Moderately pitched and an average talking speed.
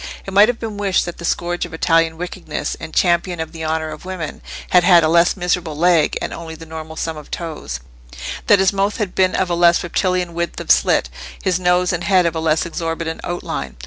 No: medium, 170 Hz; fast, 225 wpm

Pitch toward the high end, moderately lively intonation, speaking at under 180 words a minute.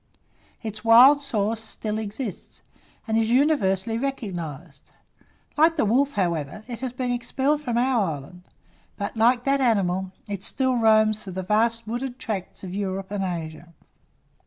Yes: high, 220 Hz; average, 4.6 semitones; average, 150 wpm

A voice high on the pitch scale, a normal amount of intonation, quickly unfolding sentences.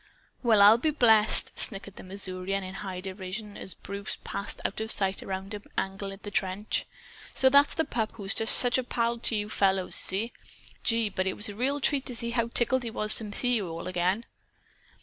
Yes: high, 210 Hz; average, 3.3 semitones; fast, 210 wpm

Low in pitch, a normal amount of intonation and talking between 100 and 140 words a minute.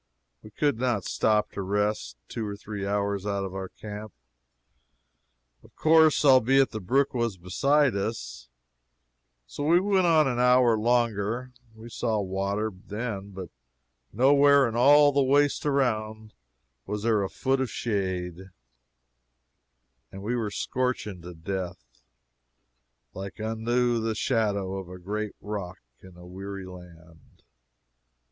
Yes: low, 110 Hz; average, 4.3 semitones; slow, 135 wpm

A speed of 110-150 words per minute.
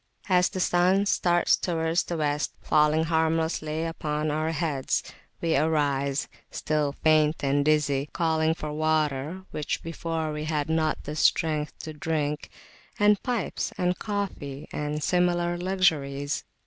Yes: slow, 135 wpm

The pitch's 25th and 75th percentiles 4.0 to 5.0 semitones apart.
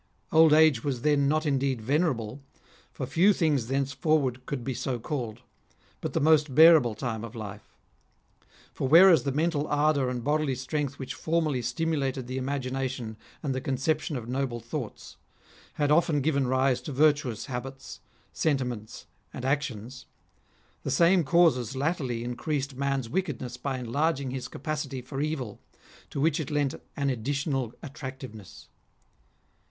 No: average, 3.2 semitones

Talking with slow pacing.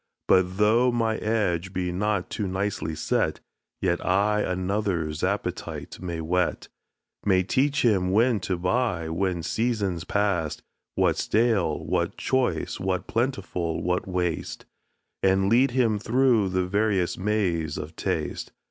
Yes: slow, 130 wpm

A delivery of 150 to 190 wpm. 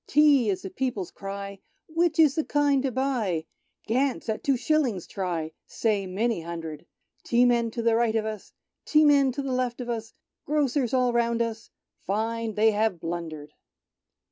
Yes: average, 160 wpm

